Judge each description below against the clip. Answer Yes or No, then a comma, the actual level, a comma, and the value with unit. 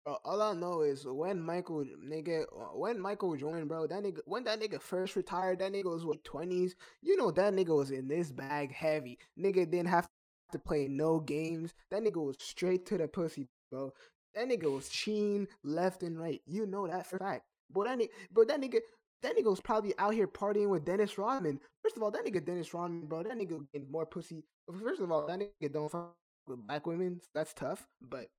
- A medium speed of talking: No, fast, 220 wpm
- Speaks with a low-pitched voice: No, medium, 175 Hz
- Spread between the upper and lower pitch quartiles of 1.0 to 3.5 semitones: No, average, 4.3 semitones